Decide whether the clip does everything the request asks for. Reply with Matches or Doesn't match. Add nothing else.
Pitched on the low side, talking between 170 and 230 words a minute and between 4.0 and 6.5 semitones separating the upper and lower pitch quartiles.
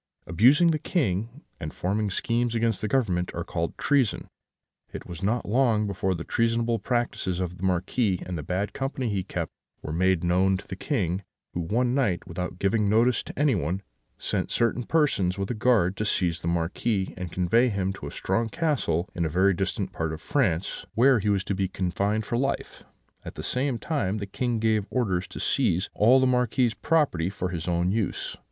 Matches